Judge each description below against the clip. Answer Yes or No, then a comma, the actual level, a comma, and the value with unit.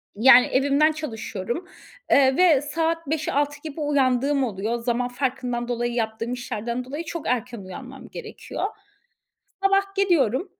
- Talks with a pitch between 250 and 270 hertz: Yes, very high, 265 Hz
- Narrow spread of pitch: No, average, 4.3 semitones